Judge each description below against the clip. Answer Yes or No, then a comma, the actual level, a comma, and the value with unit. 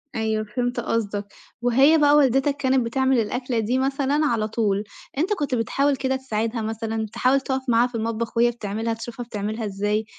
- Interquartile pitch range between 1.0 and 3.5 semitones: Yes, average, 3.2 semitones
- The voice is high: Yes, high, 235 Hz